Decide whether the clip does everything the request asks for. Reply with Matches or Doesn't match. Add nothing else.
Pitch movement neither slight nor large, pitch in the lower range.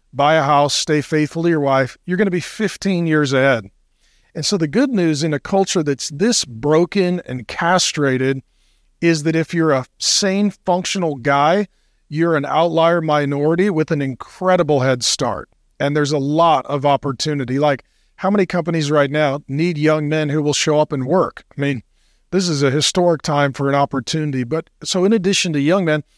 Doesn't match